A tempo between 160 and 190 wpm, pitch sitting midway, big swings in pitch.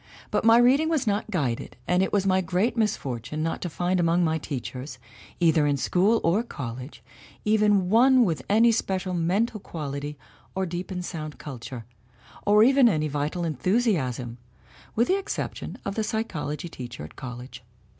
Yes: average, 165 wpm; medium, 180 Hz; wide, 6.5 semitones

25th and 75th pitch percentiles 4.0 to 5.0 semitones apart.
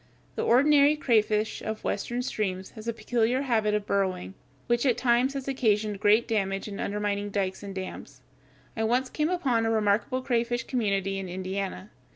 No: average, 3.5 semitones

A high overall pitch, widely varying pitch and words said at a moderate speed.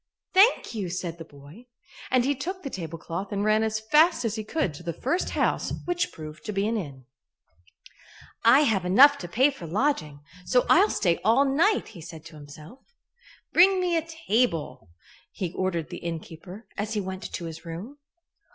Yes: high, 210 Hz; wide, 8.5 semitones; average, 185 wpm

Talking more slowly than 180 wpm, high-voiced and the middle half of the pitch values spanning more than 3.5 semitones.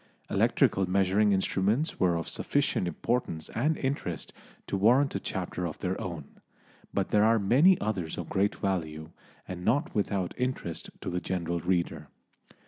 No: average, 150 wpm; very low, 95 Hz; average, 4.2 semitones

